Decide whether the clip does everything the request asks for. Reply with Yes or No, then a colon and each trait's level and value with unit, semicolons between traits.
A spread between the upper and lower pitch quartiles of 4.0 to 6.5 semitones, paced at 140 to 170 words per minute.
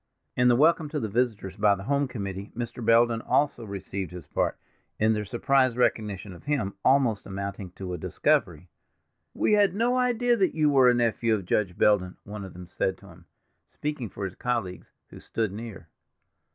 No: average, 5.1 semitones; average, 190 wpm